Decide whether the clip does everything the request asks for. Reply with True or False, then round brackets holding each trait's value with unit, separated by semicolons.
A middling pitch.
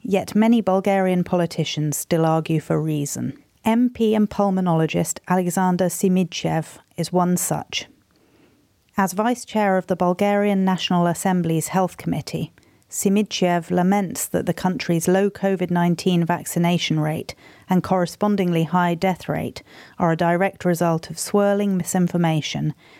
True (180 Hz)